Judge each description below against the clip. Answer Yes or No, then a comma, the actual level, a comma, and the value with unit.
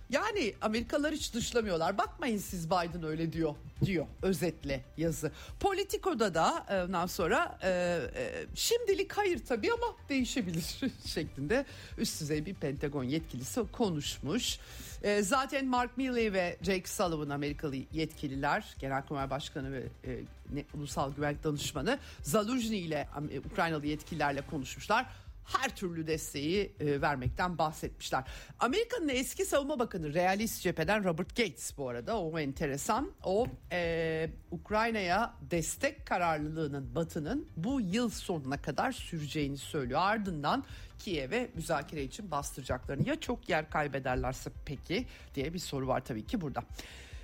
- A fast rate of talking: No, average, 120 wpm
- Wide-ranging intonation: Yes, wide, 8.0 semitones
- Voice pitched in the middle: Yes, medium, 170 Hz